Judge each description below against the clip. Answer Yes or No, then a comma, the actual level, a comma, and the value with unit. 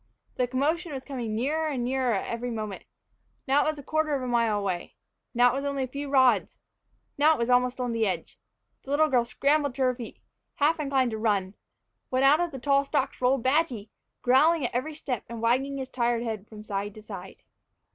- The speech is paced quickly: Yes, fast, 215 wpm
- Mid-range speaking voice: No, very high, 255 Hz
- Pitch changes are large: No, average, 3.3 semitones